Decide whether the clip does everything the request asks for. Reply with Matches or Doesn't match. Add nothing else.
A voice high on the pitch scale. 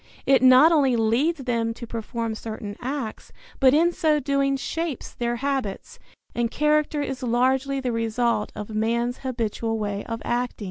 Matches